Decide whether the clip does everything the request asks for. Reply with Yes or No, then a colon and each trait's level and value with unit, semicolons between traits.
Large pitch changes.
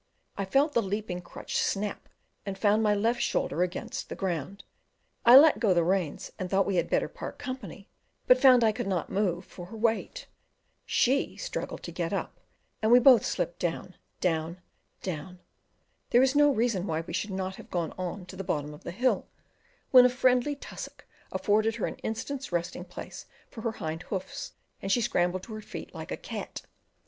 No: average, 5.0 semitones